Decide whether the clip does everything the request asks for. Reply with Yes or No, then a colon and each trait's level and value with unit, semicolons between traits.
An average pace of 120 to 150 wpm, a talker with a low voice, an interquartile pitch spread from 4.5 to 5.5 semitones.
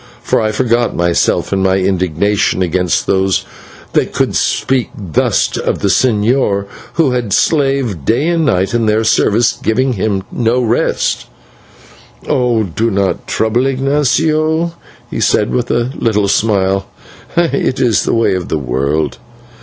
Yes: average, 140 wpm; low, 110 Hz; average, 5.0 semitones